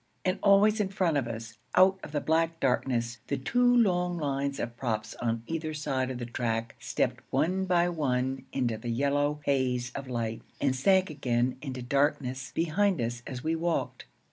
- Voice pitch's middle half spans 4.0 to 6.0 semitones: Yes, wide, 5.5 semitones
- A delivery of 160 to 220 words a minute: Yes, average, 180 wpm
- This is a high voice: No, medium, 140 Hz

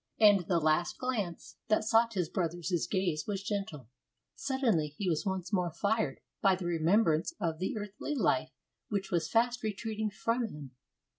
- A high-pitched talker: Yes, high, 195 Hz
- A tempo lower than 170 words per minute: Yes, average, 160 wpm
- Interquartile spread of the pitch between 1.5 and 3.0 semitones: No, average, 4.3 semitones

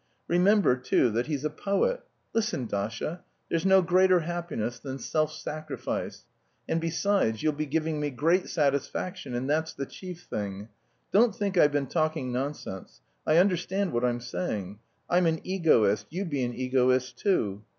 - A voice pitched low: No, medium, 155 Hz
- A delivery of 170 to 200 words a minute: No, average, 160 wpm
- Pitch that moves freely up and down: Yes, wide, 6.1 semitones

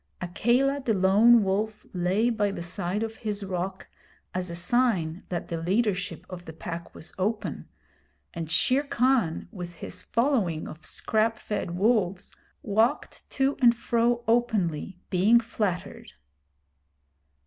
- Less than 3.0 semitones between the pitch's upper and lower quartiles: No, average, 4.9 semitones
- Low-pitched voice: No, high, 205 Hz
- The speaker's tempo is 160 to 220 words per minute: No, slow, 135 wpm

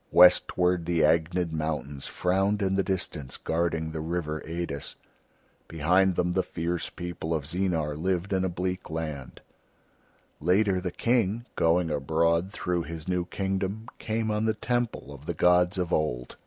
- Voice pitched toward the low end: Yes, very low, 90 Hz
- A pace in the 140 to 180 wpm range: Yes, average, 155 wpm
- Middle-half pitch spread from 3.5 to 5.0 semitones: No, average, 2.9 semitones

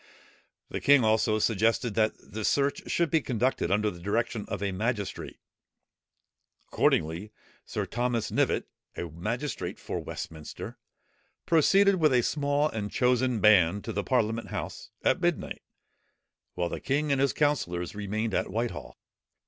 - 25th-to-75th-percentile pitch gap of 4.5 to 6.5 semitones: Yes, average, 4.8 semitones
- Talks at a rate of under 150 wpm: Yes, average, 140 wpm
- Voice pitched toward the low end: Yes, low, 115 Hz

